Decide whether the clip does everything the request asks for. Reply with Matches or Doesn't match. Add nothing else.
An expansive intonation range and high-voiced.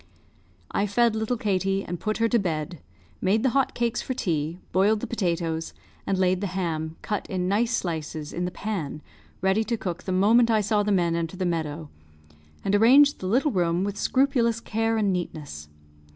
Doesn't match